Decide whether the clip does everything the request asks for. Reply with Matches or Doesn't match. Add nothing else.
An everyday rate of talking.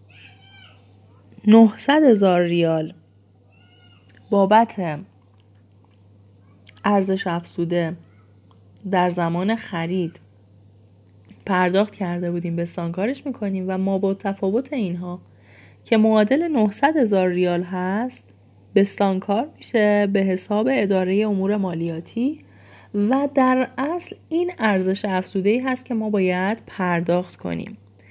Doesn't match